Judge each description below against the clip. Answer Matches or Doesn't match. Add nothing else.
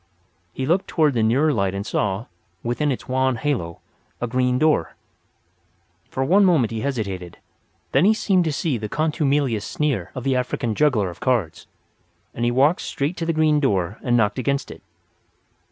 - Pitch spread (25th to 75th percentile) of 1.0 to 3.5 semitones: Doesn't match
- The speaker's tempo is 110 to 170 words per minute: Doesn't match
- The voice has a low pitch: Matches